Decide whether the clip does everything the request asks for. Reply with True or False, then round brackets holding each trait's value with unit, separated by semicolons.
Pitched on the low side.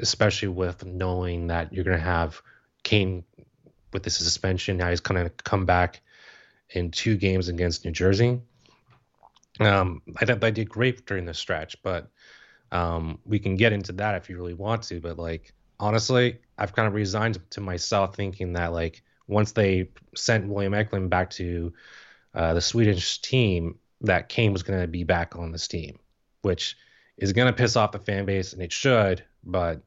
True (95 Hz)